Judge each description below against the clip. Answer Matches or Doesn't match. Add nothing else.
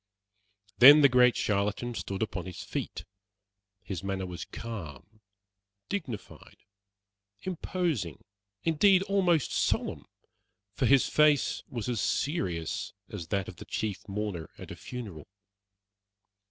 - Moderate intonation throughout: Doesn't match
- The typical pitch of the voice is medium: Doesn't match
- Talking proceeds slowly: Matches